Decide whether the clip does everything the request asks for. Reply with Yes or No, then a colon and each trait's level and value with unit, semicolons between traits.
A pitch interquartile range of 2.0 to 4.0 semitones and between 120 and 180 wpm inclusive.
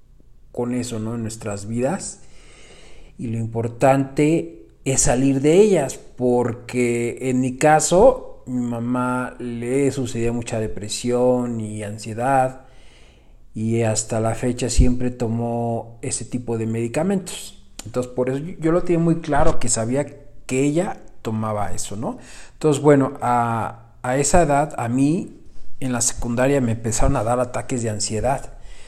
Yes: average, 3.0 semitones; average, 140 wpm